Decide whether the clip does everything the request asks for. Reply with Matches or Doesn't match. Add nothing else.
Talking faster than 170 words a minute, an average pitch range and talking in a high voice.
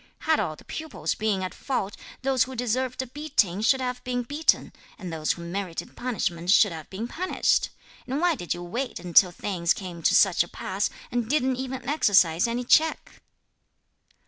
Doesn't match